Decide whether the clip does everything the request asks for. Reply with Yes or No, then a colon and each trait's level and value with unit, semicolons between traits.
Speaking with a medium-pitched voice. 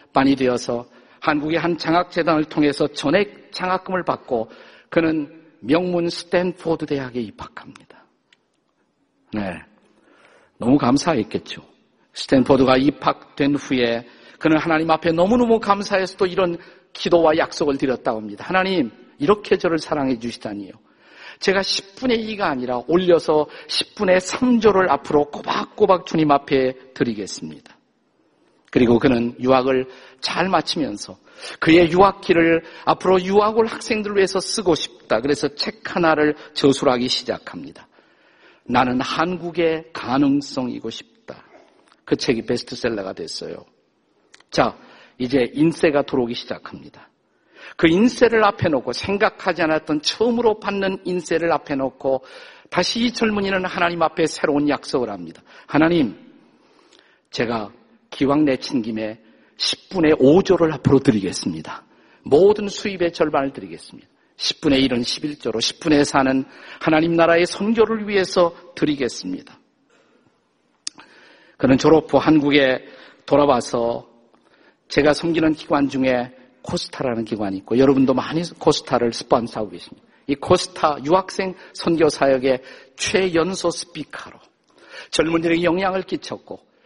Yes: medium, 160 Hz